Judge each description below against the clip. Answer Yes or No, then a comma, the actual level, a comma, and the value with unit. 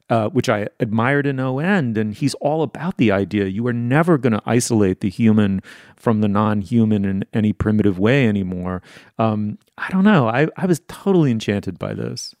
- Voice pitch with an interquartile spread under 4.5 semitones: No, average, 5.1 semitones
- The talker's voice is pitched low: Yes, low, 110 Hz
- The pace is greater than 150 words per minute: Yes, average, 200 wpm